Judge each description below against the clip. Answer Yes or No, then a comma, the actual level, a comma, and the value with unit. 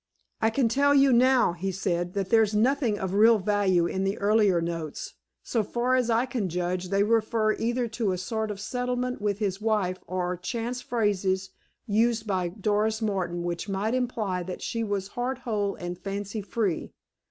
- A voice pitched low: No, high, 210 Hz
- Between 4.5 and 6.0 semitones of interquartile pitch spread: No, average, 3.6 semitones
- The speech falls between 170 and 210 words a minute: Yes, average, 180 wpm